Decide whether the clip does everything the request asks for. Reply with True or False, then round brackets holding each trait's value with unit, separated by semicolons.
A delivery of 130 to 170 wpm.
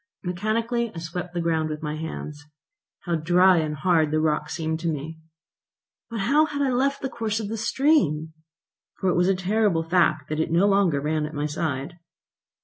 False (195 wpm)